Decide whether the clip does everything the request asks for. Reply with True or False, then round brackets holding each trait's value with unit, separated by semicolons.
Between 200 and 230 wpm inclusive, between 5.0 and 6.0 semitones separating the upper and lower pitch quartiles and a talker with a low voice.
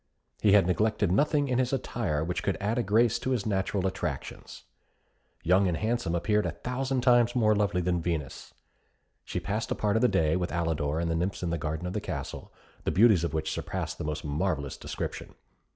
True (205 wpm; 5.3 semitones; 95 Hz)